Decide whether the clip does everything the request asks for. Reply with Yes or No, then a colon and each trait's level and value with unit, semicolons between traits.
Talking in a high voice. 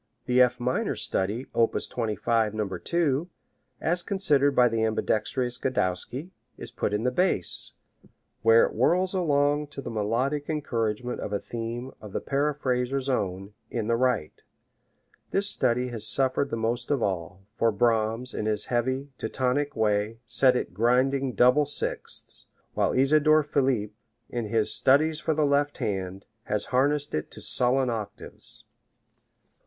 No: low, 125 Hz